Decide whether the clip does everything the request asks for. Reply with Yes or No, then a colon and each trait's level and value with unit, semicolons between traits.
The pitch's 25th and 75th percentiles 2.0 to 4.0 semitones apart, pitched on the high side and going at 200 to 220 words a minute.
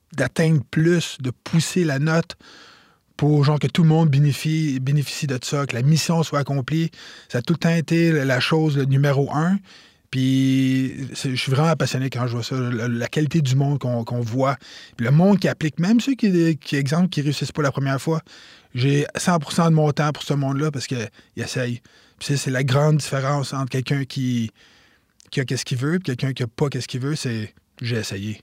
No: average, 3.4 semitones; medium, 140 Hz; average, 215 wpm